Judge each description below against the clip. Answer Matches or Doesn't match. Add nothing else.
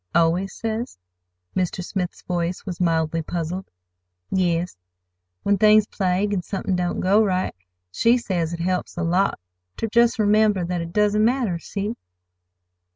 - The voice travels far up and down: Doesn't match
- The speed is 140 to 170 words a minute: Matches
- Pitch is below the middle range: Doesn't match